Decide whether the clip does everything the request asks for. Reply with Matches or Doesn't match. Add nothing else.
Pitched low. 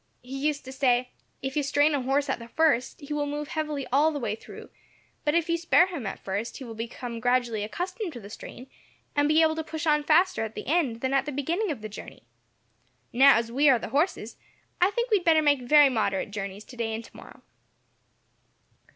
Doesn't match